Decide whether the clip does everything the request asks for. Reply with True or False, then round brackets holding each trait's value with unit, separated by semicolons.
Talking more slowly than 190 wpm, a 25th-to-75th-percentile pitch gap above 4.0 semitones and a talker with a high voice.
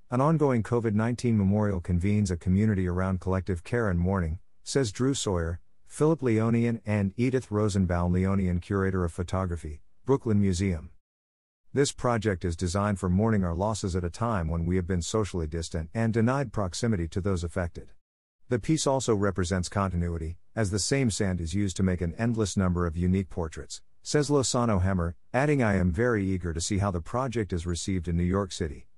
False (180 wpm; 4.4 semitones; 95 Hz)